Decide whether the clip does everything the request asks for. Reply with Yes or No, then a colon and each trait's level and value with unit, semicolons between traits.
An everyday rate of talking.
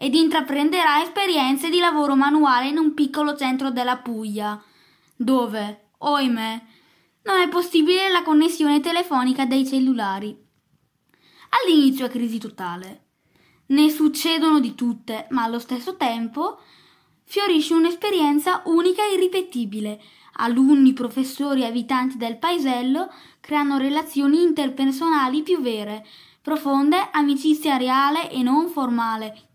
No: slow, 110 wpm